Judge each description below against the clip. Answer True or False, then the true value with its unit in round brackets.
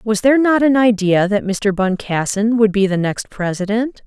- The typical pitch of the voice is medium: False (215 Hz)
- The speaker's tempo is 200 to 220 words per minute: False (190 wpm)